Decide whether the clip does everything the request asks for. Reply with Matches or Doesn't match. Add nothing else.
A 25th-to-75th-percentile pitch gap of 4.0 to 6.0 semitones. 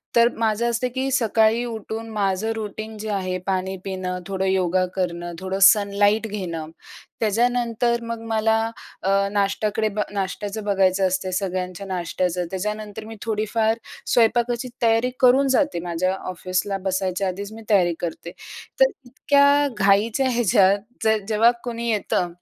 Doesn't match